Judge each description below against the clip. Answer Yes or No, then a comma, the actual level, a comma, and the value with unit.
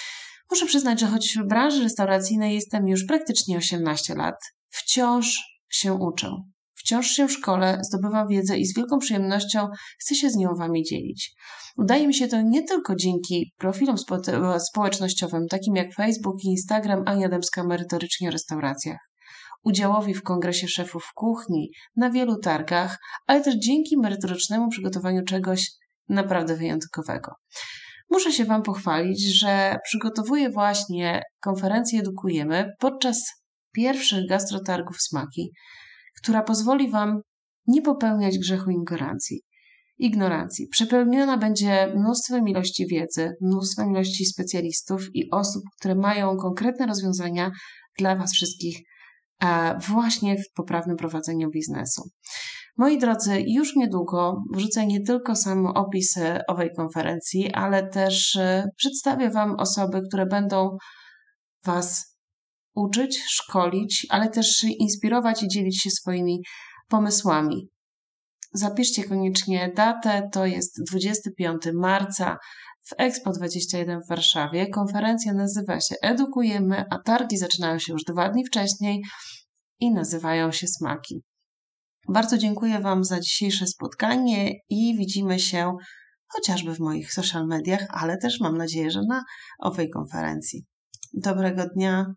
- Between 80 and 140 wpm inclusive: Yes, average, 125 wpm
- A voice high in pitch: Yes, high, 195 Hz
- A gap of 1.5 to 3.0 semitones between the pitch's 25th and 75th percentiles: No, average, 3.9 semitones